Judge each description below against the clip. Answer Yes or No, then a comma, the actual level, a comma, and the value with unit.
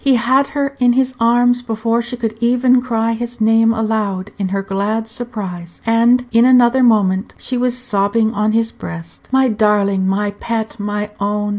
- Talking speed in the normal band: Yes, average, 175 wpm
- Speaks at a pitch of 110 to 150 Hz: No, high, 225 Hz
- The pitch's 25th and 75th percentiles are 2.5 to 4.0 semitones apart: Yes, average, 2.9 semitones